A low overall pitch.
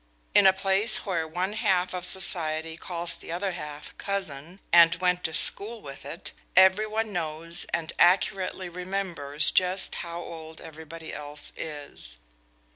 No: medium, 175 Hz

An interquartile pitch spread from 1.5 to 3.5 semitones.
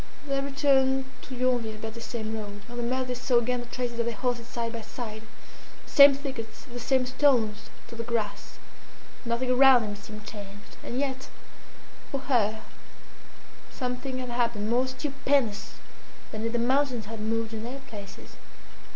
Yes: average, 2.8 semitones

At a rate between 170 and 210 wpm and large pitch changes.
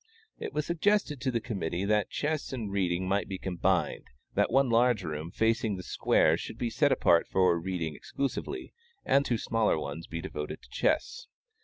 Yes: average, 180 wpm; wide, 6.7 semitones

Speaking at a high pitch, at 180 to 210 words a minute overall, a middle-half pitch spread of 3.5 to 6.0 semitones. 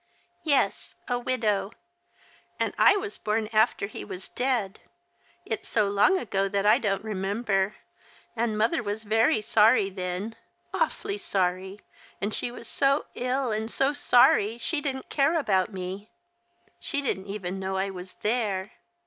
No: high, 215 Hz; average, 150 wpm; average, 4.2 semitones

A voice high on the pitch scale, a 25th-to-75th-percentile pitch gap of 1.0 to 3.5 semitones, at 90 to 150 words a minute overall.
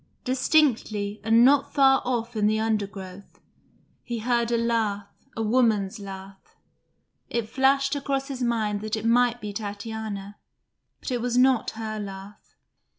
Yes: high, 225 Hz; average, 3.1 semitones; average, 145 wpm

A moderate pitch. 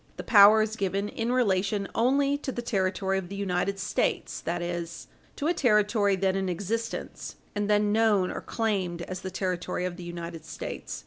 No: high, 200 Hz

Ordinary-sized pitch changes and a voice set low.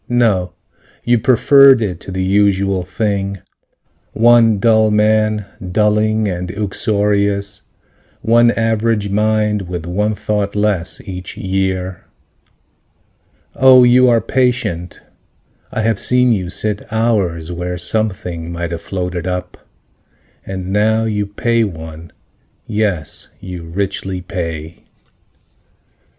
Yes: average, 3.3 semitones; low, 100 Hz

